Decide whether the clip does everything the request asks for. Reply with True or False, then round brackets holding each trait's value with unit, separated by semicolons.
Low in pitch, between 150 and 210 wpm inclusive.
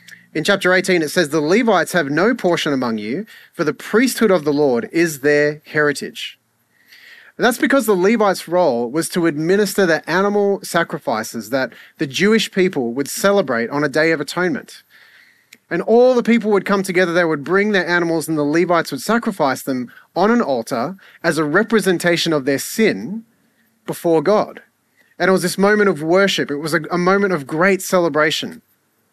False (180 Hz; 180 wpm)